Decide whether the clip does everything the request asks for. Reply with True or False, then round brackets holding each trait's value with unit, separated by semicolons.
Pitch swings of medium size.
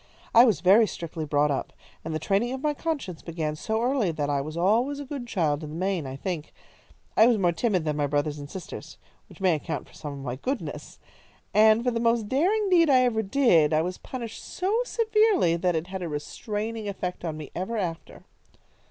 False (7.3 semitones)